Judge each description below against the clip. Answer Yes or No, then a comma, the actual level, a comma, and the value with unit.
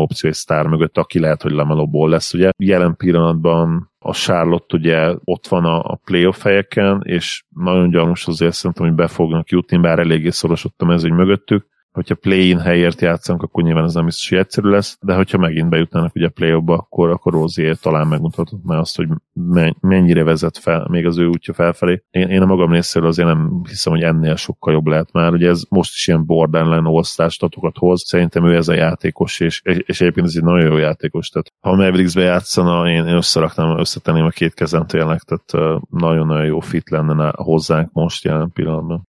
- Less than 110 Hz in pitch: Yes, very low, 85 Hz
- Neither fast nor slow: No, fast, 190 wpm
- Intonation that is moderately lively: No, narrow, 1.5 semitones